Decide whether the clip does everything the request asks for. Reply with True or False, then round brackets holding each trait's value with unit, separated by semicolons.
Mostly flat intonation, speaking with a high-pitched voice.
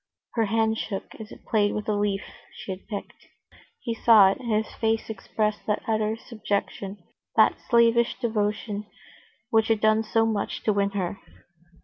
True (1.5 semitones; 215 Hz)